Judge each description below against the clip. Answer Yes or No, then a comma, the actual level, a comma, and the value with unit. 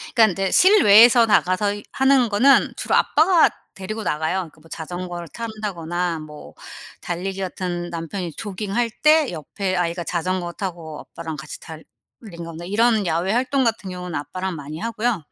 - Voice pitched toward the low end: No, medium, 185 Hz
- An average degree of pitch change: Yes, average, 4.6 semitones